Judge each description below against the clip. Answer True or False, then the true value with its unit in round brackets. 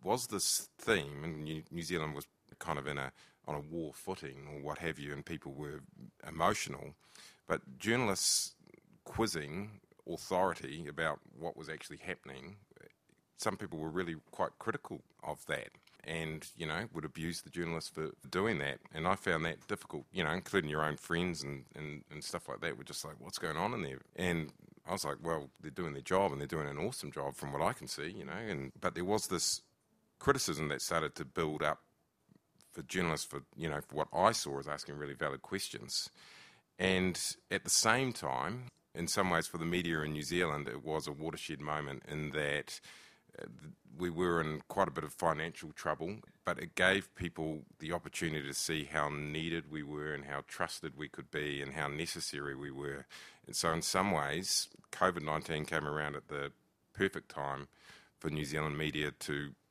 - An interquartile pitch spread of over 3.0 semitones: False (2.5 semitones)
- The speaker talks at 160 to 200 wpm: True (195 wpm)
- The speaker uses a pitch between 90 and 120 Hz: False (75 Hz)